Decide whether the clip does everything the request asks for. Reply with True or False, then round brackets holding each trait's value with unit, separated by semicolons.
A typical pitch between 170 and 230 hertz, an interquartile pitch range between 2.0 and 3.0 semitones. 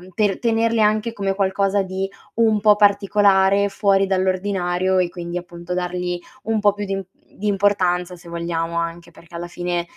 True (190 Hz; 2.5 semitones)